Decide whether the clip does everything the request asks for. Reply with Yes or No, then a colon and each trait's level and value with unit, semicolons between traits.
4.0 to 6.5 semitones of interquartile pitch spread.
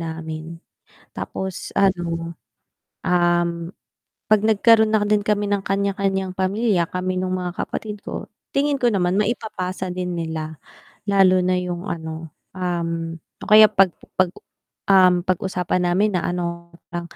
No: narrow, 2.5 semitones